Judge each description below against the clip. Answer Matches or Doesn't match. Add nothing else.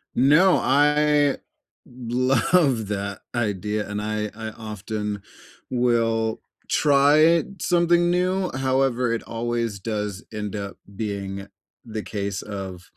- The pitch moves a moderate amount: Matches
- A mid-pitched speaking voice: Doesn't match